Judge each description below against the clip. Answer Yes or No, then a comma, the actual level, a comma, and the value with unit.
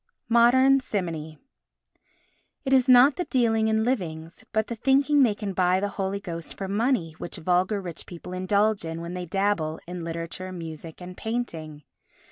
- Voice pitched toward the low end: No, high, 195 Hz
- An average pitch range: No, wide, 5.7 semitones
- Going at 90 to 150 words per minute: No, average, 165 wpm